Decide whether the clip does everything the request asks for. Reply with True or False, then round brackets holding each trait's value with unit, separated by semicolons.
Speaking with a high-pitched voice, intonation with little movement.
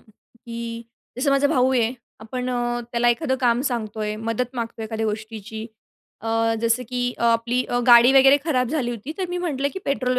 True (240 Hz; 2.1 semitones)